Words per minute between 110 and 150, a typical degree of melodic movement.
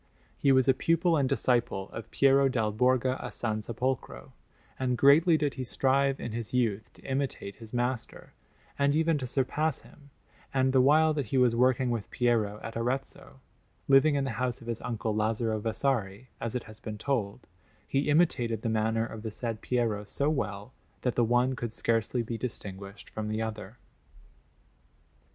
No: average, 180 wpm; average, 3.4 semitones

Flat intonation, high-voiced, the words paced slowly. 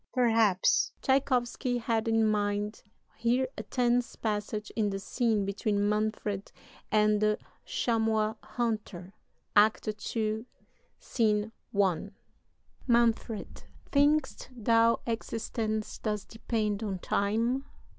Yes: narrow, 2.0 semitones; high, 220 Hz; slow, 100 wpm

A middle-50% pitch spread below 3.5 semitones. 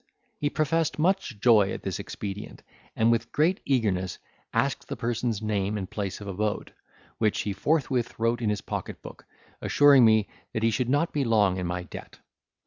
No: average, 4.7 semitones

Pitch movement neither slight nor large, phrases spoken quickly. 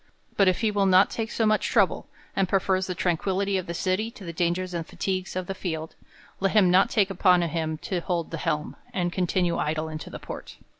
No: narrow, 2.3 semitones; fast, 220 wpm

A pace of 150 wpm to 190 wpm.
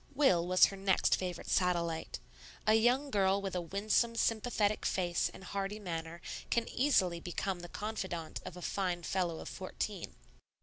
Yes: average, 160 wpm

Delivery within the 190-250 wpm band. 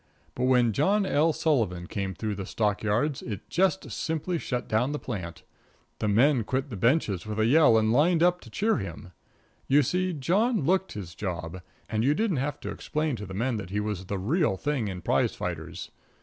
Yes: fast, 205 wpm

